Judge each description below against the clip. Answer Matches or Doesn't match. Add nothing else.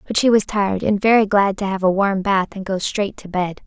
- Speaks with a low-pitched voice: Doesn't match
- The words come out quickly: Matches